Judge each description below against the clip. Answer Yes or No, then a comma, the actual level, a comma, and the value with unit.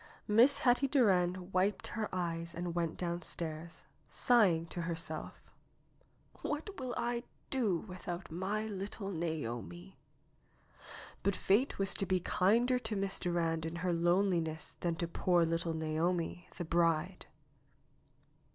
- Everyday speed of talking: No, slow, 130 wpm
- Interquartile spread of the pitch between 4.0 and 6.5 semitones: No, average, 3.3 semitones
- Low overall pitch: No, medium, 180 Hz